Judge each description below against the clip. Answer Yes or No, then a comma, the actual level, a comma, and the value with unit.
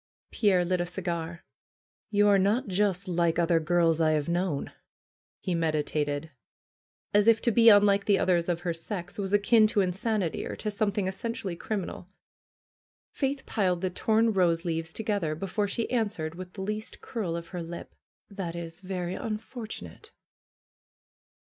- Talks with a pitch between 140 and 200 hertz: Yes, medium, 185 Hz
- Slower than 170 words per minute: Yes, average, 160 wpm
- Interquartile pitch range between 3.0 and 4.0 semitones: Yes, average, 3.5 semitones